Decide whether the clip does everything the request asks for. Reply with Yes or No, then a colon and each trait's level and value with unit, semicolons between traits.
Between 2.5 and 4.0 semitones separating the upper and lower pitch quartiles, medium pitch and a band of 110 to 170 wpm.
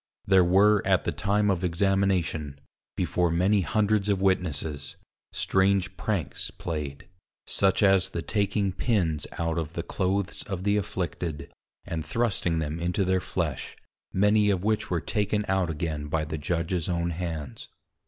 No: average, 3.3 semitones; very low, 90 Hz; average, 150 wpm